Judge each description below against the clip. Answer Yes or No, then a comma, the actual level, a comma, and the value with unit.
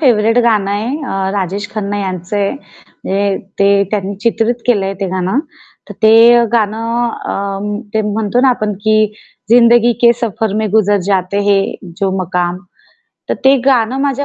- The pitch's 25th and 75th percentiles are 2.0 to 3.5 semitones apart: Yes, average, 3.0 semitones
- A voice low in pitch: No, high, 210 Hz